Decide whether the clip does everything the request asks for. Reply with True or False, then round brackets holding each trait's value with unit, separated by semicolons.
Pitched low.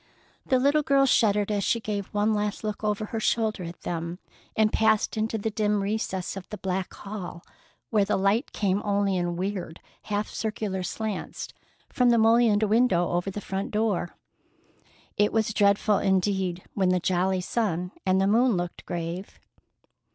False (205 Hz)